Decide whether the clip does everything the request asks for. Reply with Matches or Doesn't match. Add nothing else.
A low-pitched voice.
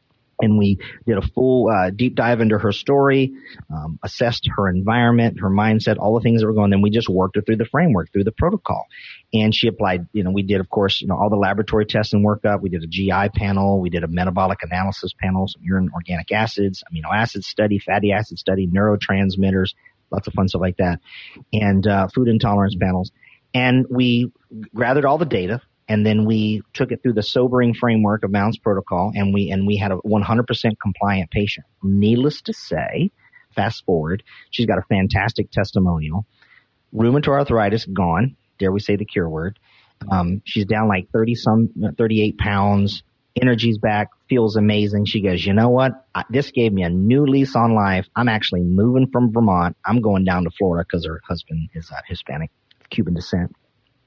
Matches